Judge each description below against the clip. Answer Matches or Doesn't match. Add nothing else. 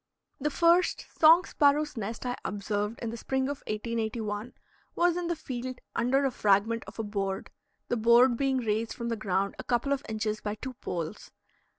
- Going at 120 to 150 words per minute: Doesn't match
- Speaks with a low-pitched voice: Doesn't match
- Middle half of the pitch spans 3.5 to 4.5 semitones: Matches